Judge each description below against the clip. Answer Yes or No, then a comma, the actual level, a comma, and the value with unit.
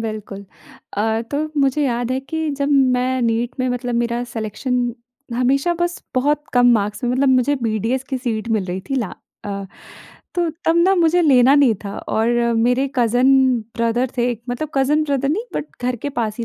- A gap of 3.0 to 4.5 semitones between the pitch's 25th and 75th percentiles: Yes, average, 3.3 semitones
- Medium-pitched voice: No, very high, 250 Hz